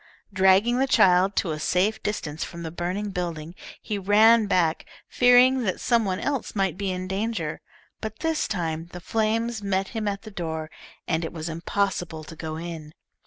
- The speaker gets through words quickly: No, average, 180 wpm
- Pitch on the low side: No, high, 190 Hz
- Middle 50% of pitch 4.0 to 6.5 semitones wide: Yes, average, 4.5 semitones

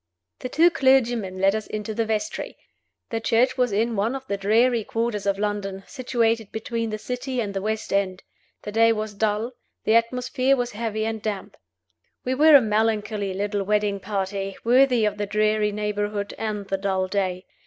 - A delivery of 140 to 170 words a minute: No, average, 180 wpm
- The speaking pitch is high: Yes, high, 215 Hz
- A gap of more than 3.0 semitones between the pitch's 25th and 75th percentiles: No, narrow, 2.5 semitones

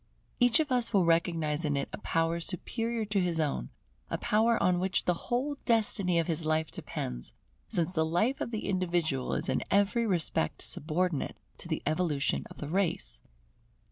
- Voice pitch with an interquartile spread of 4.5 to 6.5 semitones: Yes, average, 4.9 semitones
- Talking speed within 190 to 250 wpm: No, average, 180 wpm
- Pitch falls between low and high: Yes, medium, 175 Hz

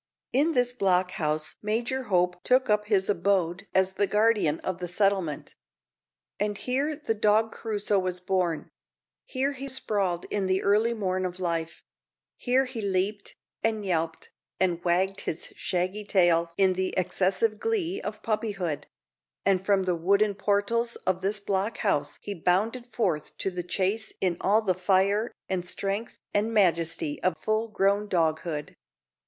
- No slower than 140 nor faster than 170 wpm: Yes, average, 155 wpm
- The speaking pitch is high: Yes, high, 195 Hz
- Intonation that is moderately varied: Yes, average, 3.2 semitones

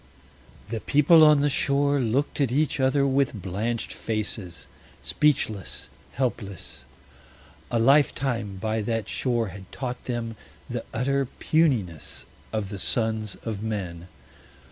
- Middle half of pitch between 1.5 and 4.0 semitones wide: No, average, 4.7 semitones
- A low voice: Yes, low, 115 Hz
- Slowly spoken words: Yes, slow, 120 wpm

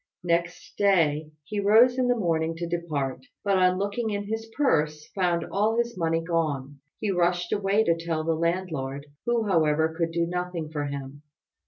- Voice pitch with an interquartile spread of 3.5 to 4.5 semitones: Yes, average, 4.1 semitones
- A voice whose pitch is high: No, medium, 170 Hz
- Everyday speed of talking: Yes, average, 175 wpm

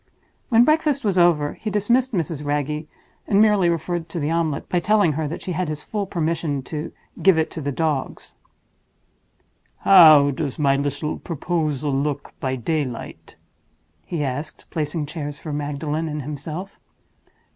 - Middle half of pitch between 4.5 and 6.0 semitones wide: No, average, 3.2 semitones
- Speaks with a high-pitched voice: No, medium, 155 Hz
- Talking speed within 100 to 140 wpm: No, average, 155 wpm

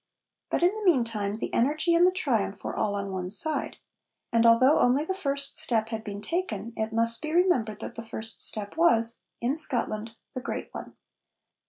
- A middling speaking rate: Yes, average, 190 wpm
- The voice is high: Yes, high, 230 Hz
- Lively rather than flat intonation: Yes, wide, 6.0 semitones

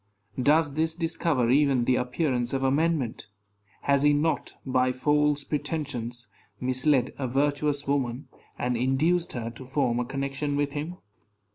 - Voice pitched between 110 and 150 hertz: Yes, medium, 140 Hz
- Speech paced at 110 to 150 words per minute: Yes, average, 140 wpm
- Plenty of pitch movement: No, average, 2.8 semitones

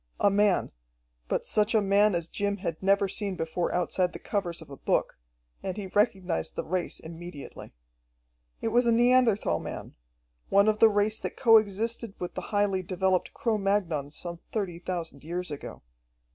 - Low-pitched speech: No, high, 195 Hz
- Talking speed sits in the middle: Yes, average, 175 wpm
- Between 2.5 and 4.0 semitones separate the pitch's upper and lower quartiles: Yes, average, 3.3 semitones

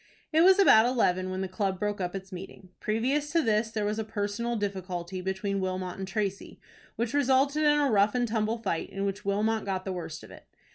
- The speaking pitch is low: No, high, 205 Hz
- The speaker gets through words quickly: Yes, fast, 220 wpm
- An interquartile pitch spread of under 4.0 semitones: Yes, average, 3.6 semitones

